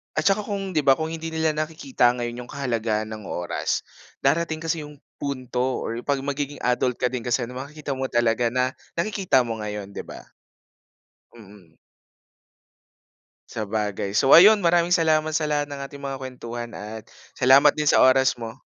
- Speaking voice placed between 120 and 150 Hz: Yes, low, 135 Hz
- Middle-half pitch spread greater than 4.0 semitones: Yes, average, 4.6 semitones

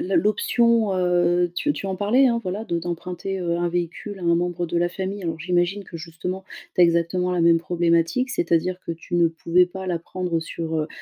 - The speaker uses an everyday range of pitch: No, narrow, 2.1 semitones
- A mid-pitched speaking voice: Yes, medium, 175 Hz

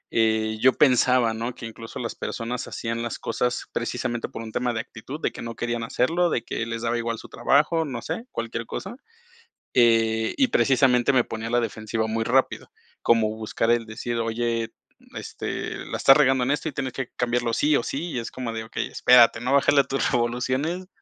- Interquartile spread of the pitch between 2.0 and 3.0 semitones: Yes, narrow, 2.4 semitones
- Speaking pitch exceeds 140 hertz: No, low, 120 Hz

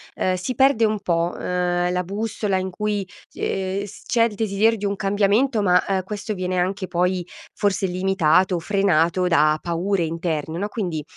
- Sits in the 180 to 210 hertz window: Yes, high, 190 Hz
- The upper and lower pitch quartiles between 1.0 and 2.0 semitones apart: No, narrow, 2.5 semitones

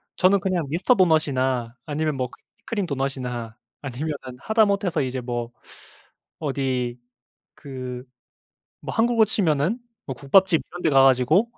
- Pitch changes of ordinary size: No, wide, 6.2 semitones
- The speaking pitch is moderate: Yes, medium, 145 Hz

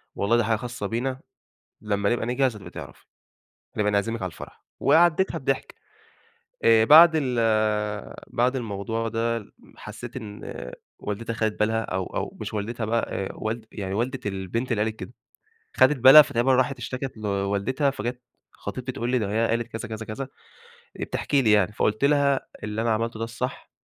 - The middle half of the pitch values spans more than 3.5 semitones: No, average, 3.0 semitones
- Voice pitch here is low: Yes, low, 115 Hz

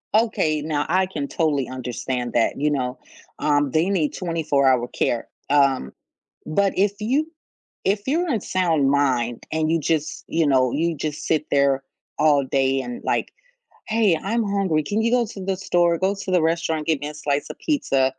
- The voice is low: No, medium, 155 Hz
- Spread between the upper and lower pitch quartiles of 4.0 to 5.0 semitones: No, wide, 5.4 semitones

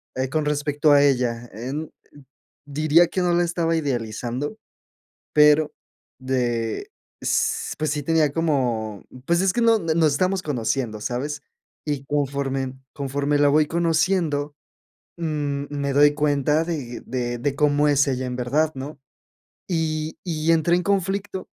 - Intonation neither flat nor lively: Yes, average, 3.4 semitones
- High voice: No, medium, 145 Hz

